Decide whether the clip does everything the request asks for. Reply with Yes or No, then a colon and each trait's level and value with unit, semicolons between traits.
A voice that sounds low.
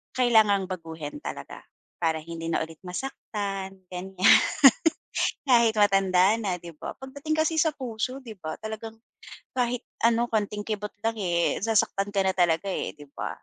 No: high, 205 Hz